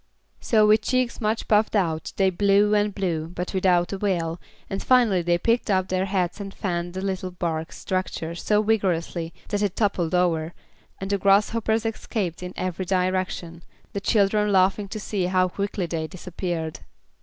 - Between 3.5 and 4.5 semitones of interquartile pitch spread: No, average, 2.9 semitones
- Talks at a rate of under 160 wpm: No, average, 165 wpm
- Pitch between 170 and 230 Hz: Yes, high, 190 Hz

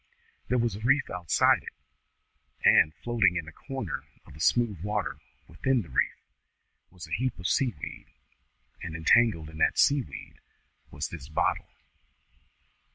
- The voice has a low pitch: Yes, low, 100 Hz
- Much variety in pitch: Yes, wide, 6.9 semitones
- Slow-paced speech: No, average, 155 wpm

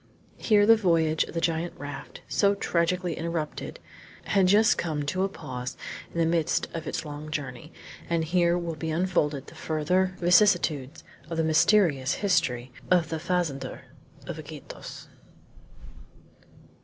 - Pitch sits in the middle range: Yes, medium, 165 Hz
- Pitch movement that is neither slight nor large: Yes, average, 3.0 semitones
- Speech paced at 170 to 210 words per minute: No, average, 145 wpm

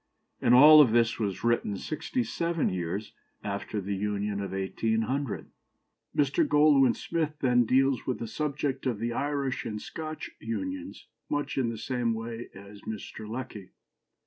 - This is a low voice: Yes, low, 120 Hz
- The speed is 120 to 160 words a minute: Yes, average, 150 wpm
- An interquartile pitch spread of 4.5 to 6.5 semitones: Yes, average, 5.2 semitones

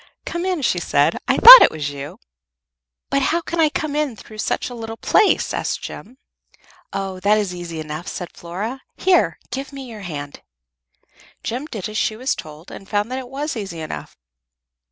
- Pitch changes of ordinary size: No, wide, 7.7 semitones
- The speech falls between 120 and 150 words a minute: No, average, 190 wpm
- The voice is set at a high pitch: Yes, high, 220 Hz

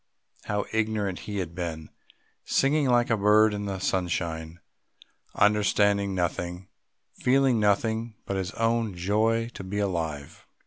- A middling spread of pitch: Yes, average, 3.7 semitones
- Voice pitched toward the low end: Yes, low, 100 Hz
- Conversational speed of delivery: No, slow, 130 wpm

